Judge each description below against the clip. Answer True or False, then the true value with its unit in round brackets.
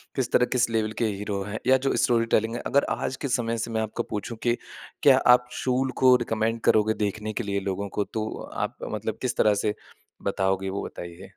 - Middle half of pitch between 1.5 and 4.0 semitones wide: True (2.9 semitones)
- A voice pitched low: True (110 Hz)